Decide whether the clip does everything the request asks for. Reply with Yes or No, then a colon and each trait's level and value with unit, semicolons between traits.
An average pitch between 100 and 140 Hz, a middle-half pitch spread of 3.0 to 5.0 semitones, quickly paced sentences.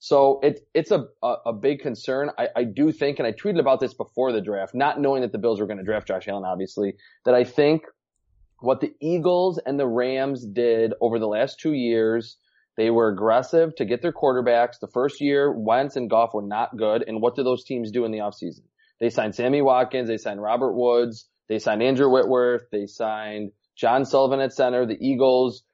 Yes: low, 125 Hz; average, 3.5 semitones; fast, 210 wpm